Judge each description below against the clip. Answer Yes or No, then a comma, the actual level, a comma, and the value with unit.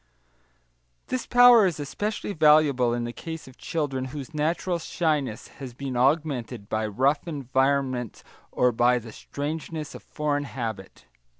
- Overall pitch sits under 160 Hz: Yes, medium, 140 Hz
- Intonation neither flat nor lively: Yes, average, 4.1 semitones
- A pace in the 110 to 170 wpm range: Yes, slow, 135 wpm